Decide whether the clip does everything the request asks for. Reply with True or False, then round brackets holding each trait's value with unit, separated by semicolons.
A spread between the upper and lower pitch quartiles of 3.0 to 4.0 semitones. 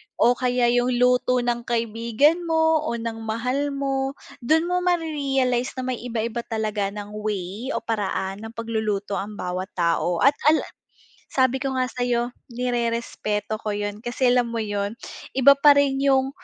True (3.7 semitones)